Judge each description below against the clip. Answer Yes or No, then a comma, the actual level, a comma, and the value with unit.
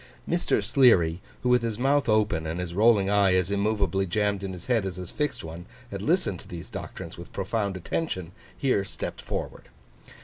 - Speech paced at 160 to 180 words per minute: No, average, 190 wpm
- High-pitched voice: No, low, 100 Hz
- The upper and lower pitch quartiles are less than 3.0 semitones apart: No, average, 3.9 semitones